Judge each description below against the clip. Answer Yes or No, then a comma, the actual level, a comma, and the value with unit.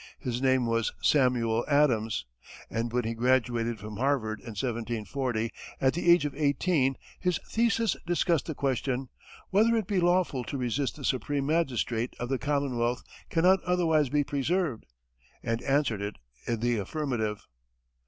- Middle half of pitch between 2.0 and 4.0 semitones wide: No, average, 4.5 semitones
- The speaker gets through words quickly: No, average, 150 wpm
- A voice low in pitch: Yes, low, 130 Hz